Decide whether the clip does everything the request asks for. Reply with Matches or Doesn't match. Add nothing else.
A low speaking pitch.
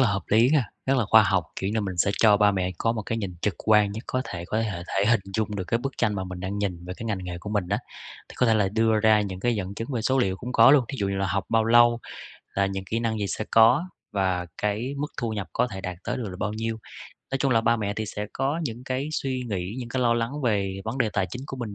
Matches